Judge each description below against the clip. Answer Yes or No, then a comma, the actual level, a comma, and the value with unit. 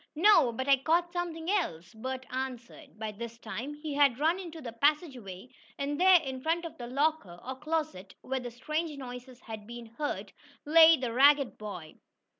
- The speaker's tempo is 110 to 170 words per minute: No, average, 180 wpm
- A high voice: Yes, very high, 265 Hz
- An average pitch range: Yes, average, 5.0 semitones